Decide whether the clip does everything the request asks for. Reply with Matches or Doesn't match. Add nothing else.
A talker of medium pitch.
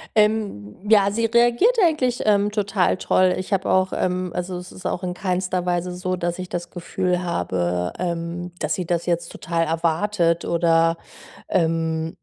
Matches